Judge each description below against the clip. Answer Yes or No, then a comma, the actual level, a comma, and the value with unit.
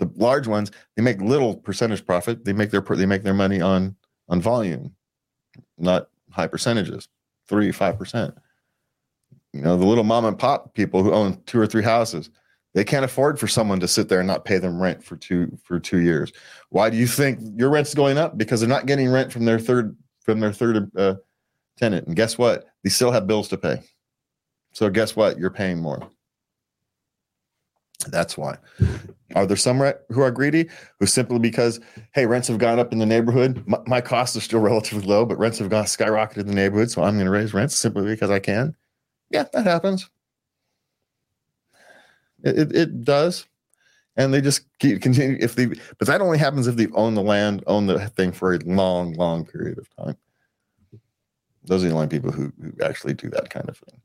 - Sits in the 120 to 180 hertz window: No, low, 110 Hz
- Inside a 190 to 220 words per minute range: Yes, average, 200 wpm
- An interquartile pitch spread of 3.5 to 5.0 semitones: Yes, average, 4.1 semitones